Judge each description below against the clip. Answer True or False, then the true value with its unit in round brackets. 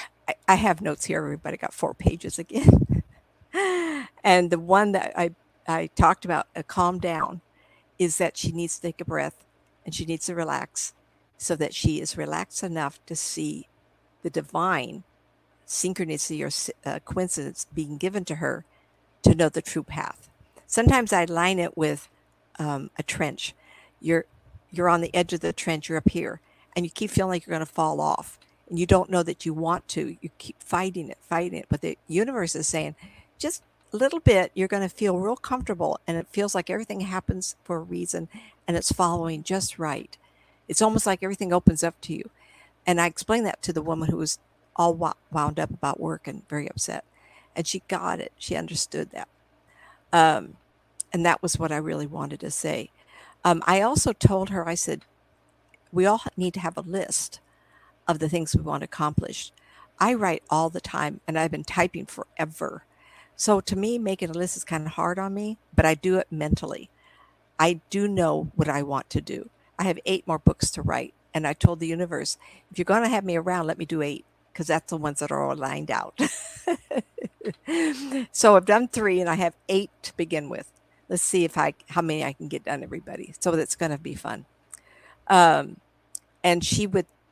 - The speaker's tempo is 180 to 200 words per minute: True (195 wpm)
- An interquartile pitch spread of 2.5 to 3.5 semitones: True (2.9 semitones)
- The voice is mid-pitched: True (175 Hz)